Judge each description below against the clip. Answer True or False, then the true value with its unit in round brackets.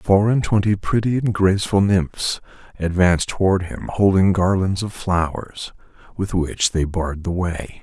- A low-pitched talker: True (95 Hz)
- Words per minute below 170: True (155 wpm)